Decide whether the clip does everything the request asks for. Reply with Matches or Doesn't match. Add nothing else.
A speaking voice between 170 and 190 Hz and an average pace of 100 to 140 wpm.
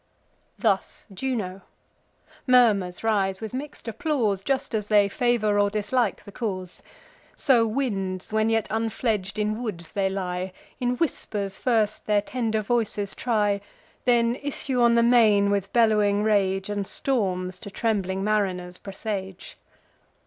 Doesn't match